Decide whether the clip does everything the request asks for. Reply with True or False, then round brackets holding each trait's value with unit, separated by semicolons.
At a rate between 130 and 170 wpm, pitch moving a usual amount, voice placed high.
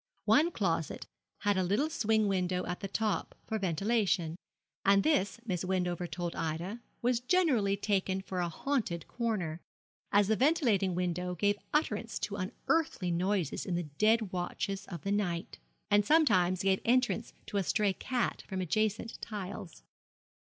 True (150 wpm; 3.6 semitones; 195 Hz)